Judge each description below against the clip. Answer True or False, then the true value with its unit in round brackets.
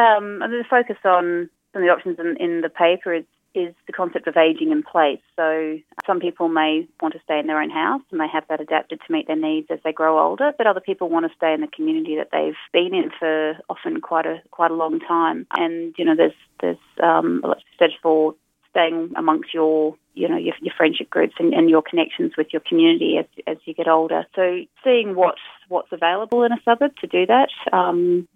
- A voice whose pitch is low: False (170 Hz)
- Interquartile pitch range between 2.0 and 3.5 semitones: False (4.0 semitones)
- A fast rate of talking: True (235 wpm)